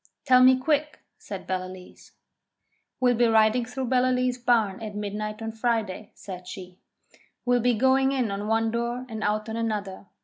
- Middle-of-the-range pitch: No, high, 225 Hz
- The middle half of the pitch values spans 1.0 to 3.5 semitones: Yes, average, 3.2 semitones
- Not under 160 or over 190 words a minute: Yes, average, 165 wpm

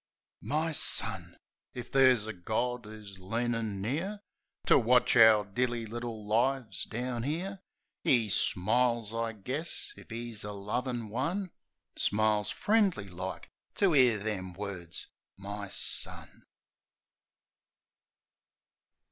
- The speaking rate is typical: No, slow, 115 wpm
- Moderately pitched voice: No, low, 115 Hz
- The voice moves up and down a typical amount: Yes, average, 3.6 semitones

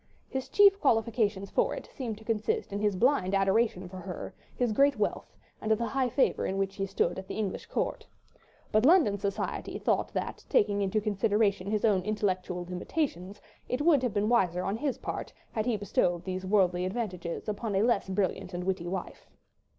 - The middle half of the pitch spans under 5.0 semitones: Yes, average, 3.7 semitones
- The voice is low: No, high, 205 Hz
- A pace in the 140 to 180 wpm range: No, average, 190 wpm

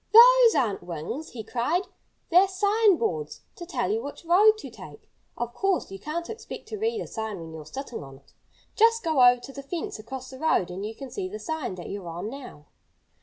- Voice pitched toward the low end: No, very high, 270 Hz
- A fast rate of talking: Yes, fast, 220 wpm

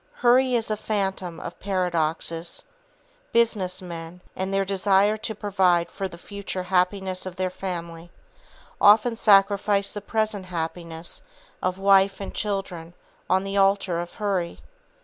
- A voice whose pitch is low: No, high, 190 Hz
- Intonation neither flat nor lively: No, narrow, 2.3 semitones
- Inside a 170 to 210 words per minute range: No, slow, 135 wpm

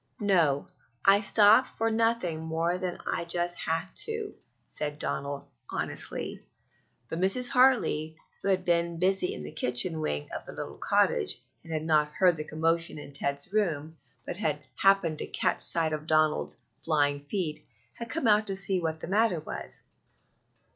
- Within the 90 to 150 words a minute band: No, average, 165 wpm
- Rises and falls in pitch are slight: No, average, 4.2 semitones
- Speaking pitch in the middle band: Yes, medium, 170 Hz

